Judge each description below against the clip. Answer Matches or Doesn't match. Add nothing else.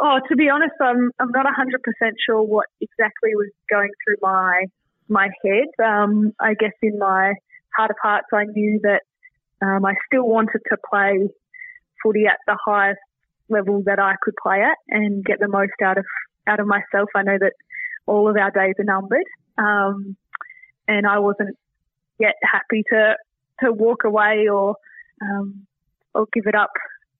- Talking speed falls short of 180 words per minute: Matches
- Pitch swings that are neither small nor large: Doesn't match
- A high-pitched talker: Matches